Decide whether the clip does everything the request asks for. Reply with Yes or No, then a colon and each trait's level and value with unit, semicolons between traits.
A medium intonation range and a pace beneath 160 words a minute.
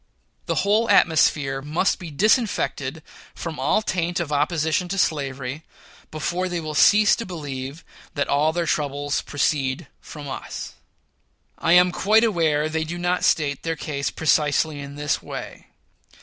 Yes: average, 3.5 semitones; average, 150 wpm